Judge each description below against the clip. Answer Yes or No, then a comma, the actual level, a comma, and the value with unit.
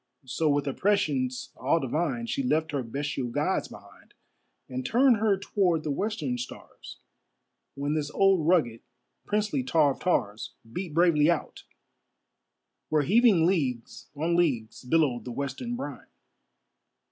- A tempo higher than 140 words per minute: No, slow, 135 wpm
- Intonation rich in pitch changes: Yes, wide, 6.1 semitones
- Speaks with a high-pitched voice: No, medium, 155 Hz